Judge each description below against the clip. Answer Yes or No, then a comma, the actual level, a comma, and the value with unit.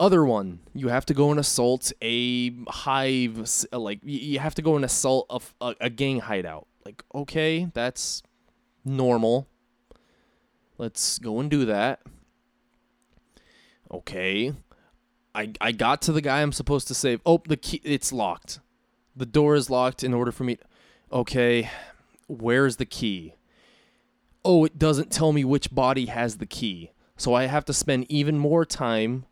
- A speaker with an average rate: Yes, average, 160 wpm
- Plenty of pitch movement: No, average, 3.4 semitones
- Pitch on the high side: No, low, 130 Hz